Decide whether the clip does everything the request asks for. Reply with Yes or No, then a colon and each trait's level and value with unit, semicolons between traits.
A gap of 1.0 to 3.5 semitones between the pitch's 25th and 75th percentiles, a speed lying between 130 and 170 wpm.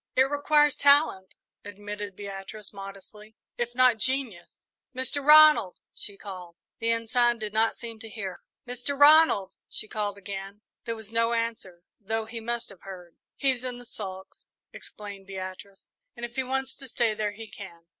No: average, 3.9 semitones; average, 165 wpm